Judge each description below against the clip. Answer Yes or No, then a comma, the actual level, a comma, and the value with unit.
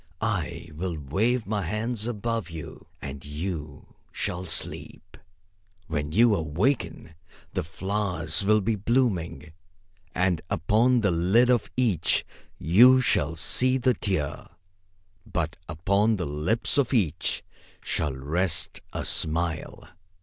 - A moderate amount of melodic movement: No, wide, 5.9 semitones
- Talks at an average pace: No, slow, 120 wpm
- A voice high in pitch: No, very low, 95 Hz